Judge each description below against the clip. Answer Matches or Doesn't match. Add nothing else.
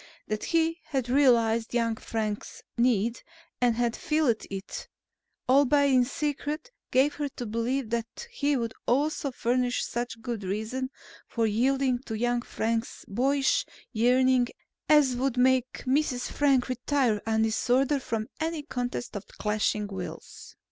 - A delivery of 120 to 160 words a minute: Matches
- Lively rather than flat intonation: Doesn't match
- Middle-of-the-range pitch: Doesn't match